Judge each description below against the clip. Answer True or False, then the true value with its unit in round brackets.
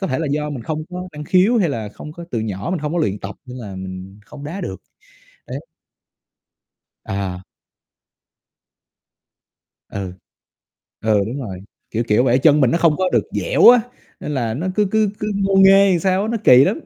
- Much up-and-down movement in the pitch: True (9.0 semitones)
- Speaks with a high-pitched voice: False (150 Hz)